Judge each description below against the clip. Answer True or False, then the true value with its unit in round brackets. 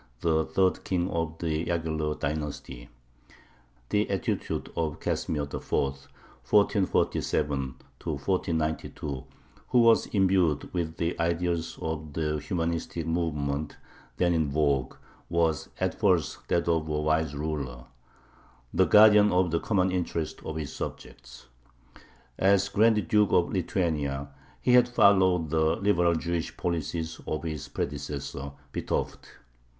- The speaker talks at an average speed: False (120 wpm)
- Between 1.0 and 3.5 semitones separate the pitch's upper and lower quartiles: True (3.0 semitones)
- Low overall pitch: True (80 Hz)